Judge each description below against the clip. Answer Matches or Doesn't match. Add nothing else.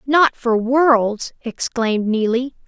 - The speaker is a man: Doesn't match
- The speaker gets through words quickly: Doesn't match